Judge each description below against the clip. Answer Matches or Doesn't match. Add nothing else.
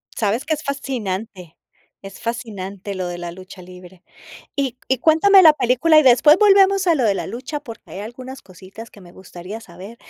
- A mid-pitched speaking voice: Doesn't match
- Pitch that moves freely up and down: Matches